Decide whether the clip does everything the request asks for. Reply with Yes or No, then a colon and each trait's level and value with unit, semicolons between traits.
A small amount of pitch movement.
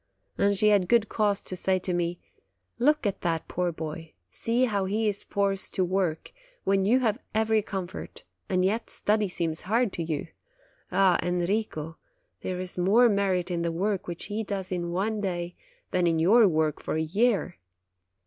No: average, 3.2 semitones